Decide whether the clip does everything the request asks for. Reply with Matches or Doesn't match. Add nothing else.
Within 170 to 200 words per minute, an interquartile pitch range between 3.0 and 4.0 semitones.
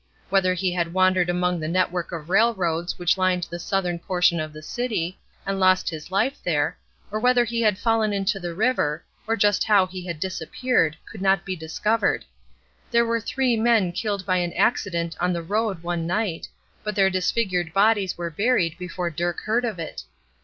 Matches